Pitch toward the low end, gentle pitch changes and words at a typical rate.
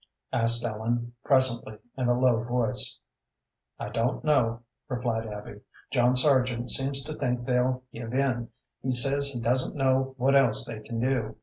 Yes: low, 125 Hz; narrow, 2.1 semitones; average, 160 wpm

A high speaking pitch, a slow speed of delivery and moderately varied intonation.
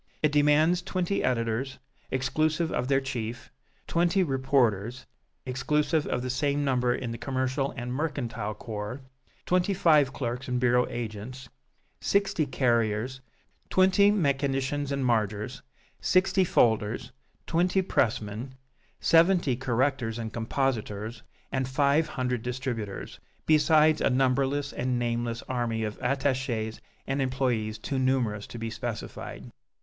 No: low, 130 Hz; slow, 120 wpm; average, 3.7 semitones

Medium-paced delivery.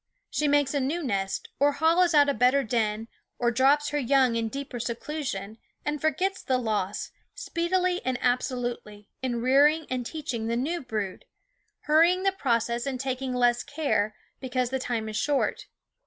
Yes: average, 170 wpm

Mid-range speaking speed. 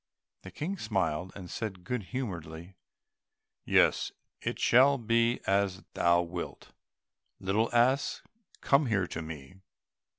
No: slow, 120 wpm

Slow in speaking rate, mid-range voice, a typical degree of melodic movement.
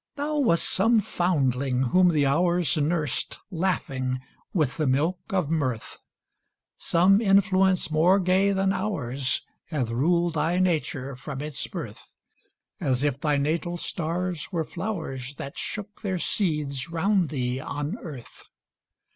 Yes: slow, 130 wpm; medium, 165 Hz; average, 4.9 semitones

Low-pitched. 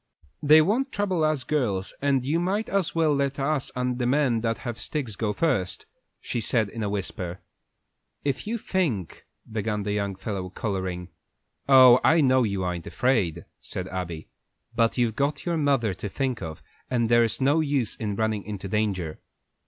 Yes: low, 120 Hz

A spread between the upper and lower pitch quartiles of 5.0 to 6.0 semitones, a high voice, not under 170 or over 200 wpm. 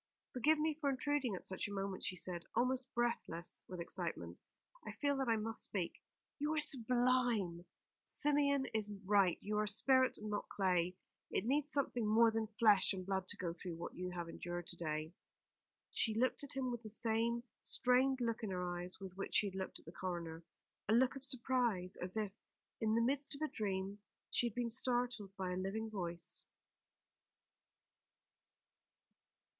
Yes: average, 5.3 semitones; high, 215 Hz; average, 180 wpm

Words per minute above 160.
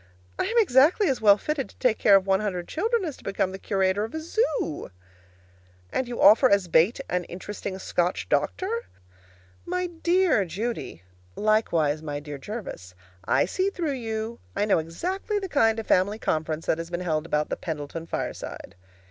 Yes: average, 180 wpm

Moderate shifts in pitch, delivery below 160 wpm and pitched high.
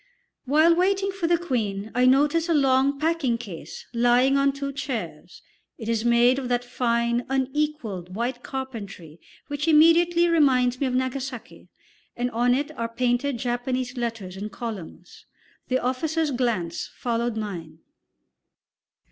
Yes: average, 3.4 semitones; average, 140 wpm; very high, 250 Hz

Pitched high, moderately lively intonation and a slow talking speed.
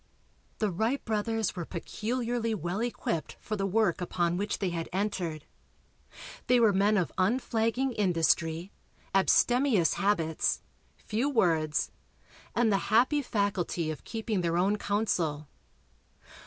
Yes: high, 200 Hz; average, 4.5 semitones; slow, 125 wpm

